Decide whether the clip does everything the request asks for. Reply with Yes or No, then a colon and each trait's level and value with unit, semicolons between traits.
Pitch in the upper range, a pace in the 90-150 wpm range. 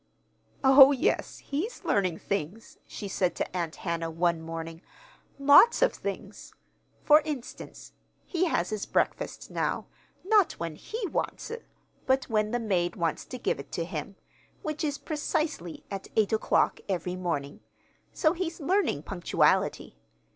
Yes: high, 215 Hz; average, 145 wpm